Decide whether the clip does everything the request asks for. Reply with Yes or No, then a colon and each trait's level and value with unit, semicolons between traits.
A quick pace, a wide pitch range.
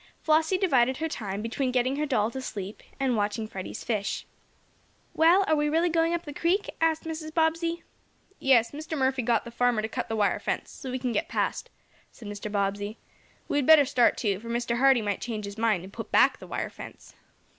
Yes: fast, 210 wpm; wide, 6.4 semitones